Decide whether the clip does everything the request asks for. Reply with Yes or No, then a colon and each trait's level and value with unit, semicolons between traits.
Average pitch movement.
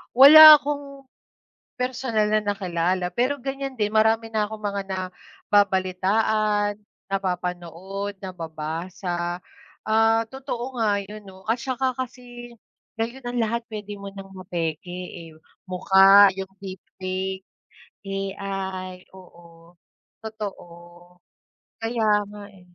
Yes: average, 3.3 semitones